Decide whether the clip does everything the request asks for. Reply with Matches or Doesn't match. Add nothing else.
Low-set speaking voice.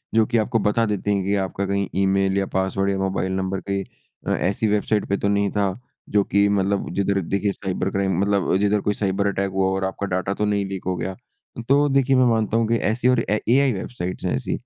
Matches